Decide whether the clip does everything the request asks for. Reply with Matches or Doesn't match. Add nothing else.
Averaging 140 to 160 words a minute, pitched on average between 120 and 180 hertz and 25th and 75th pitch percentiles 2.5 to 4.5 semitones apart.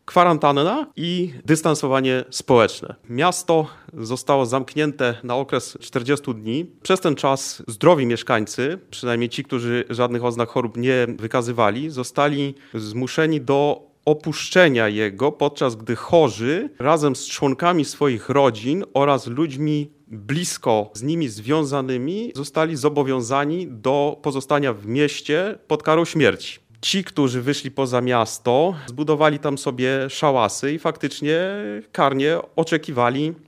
Doesn't match